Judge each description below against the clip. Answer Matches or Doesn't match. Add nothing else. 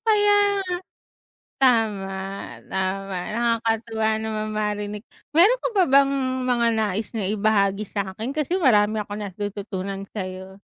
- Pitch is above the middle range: Matches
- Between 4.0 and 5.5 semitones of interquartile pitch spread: Doesn't match